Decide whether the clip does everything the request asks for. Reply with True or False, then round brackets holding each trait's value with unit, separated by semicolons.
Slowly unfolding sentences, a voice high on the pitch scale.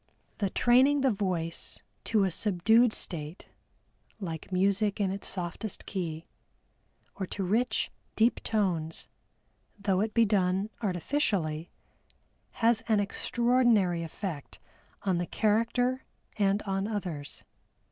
True (115 wpm; 200 Hz)